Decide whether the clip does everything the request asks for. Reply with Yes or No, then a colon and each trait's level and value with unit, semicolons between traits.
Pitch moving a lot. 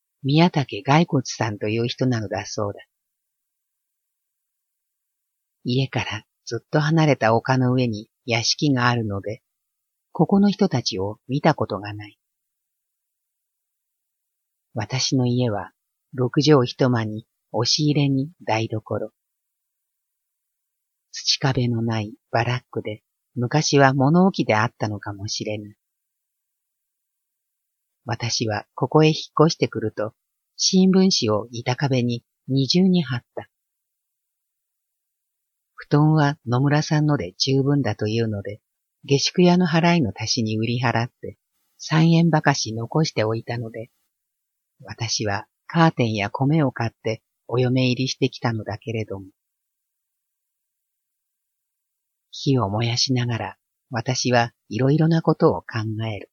No: average, 4.7 semitones